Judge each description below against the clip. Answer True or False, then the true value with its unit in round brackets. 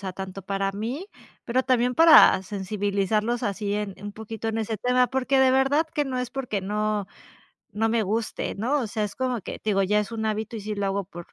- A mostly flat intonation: False (3.8 semitones)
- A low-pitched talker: False (215 Hz)